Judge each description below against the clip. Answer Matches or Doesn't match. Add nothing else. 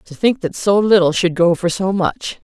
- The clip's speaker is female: Matches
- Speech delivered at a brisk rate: Matches